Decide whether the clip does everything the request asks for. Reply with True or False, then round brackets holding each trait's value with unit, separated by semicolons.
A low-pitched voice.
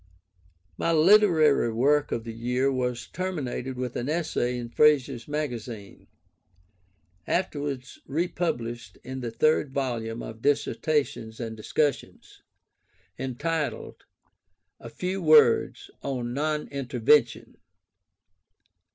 True (130 Hz)